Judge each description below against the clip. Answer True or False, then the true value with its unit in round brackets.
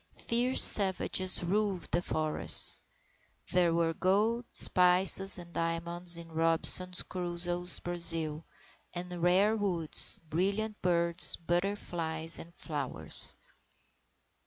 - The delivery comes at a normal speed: False (95 wpm)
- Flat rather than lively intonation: True (2.1 semitones)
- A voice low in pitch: False (175 Hz)